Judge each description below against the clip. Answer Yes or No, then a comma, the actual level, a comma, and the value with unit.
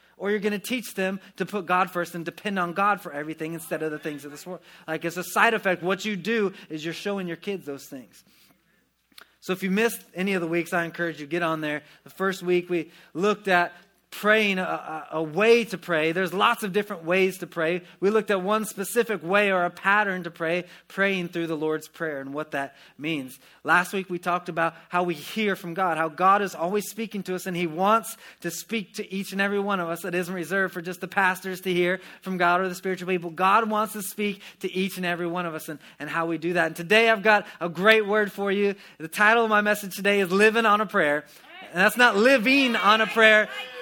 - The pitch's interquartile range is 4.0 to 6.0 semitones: No, average, 3.3 semitones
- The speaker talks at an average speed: No, fast, 245 wpm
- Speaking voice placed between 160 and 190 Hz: Yes, medium, 185 Hz